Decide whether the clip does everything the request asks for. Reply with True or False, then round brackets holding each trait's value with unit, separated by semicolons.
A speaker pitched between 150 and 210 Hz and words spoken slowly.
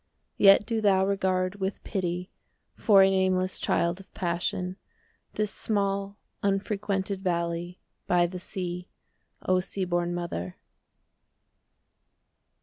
True (190 Hz; 115 wpm)